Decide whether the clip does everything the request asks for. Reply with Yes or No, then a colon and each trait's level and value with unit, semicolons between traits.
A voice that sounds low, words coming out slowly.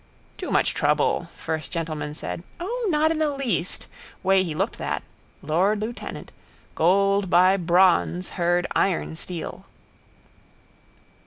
No: medium, 185 Hz; slow, 125 wpm